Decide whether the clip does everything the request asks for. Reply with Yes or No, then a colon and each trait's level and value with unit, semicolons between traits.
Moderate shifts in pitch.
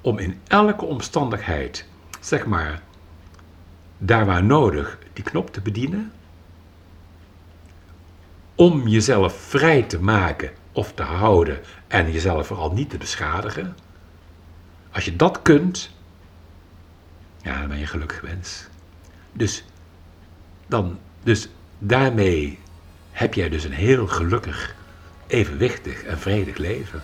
Yes: average, 3.1 semitones